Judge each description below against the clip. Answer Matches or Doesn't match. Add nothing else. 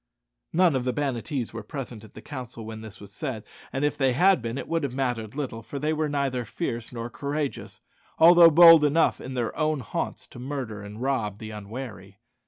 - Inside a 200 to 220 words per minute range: Matches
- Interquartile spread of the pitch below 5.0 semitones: Matches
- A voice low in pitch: Matches